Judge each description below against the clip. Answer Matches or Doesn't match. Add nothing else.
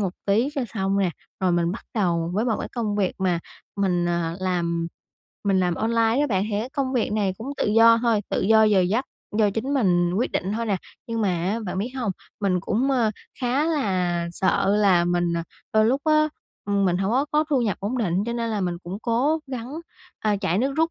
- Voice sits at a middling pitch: Doesn't match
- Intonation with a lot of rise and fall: Doesn't match